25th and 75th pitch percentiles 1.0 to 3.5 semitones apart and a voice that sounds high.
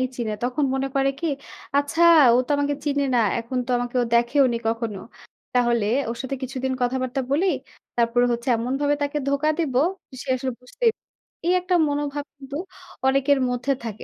Yes: average, 2.8 semitones; very high, 265 Hz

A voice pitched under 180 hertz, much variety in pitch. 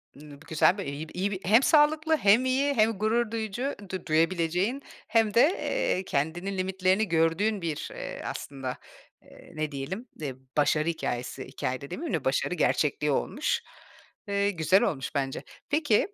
No: high, 190 Hz; wide, 6.5 semitones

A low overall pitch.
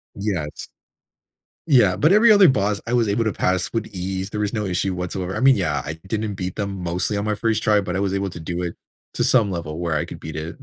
Yes: low, 100 Hz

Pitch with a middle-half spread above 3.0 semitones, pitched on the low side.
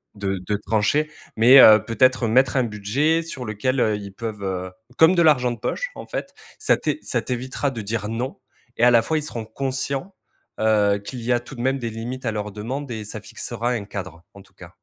Yes: average, 3.9 semitones; low, 115 Hz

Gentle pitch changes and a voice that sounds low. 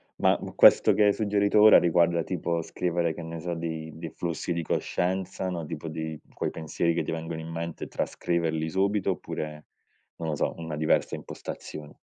Yes: narrow, 1.8 semitones; very low, 85 Hz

